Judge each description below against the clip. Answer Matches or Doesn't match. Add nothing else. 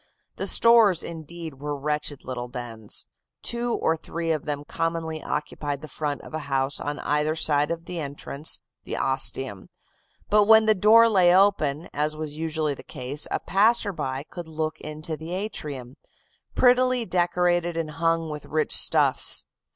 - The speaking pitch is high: Doesn't match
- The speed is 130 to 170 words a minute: Matches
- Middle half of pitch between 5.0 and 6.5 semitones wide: Doesn't match